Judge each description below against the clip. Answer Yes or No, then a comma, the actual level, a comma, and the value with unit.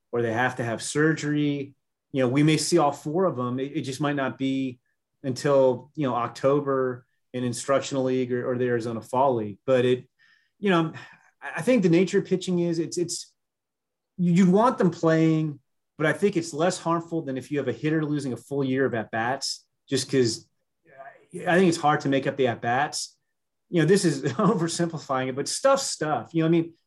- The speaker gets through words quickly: Yes, fast, 210 wpm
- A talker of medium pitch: Yes, medium, 145 Hz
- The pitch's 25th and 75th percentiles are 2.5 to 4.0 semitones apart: No, average, 4.5 semitones